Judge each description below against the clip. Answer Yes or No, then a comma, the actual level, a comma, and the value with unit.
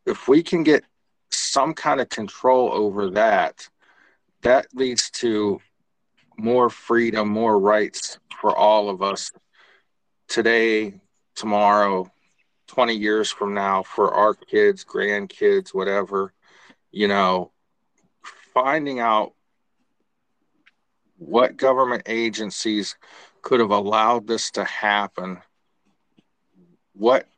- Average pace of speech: No, slow, 100 wpm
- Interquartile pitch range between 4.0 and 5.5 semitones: No, average, 3.5 semitones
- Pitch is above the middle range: No, low, 110 Hz